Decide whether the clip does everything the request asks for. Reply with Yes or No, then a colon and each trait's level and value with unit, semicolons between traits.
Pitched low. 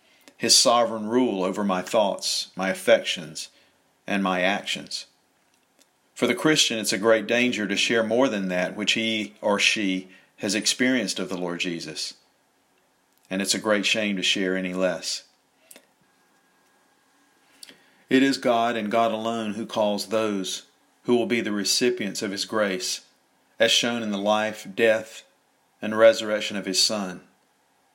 Yes: low, 110 Hz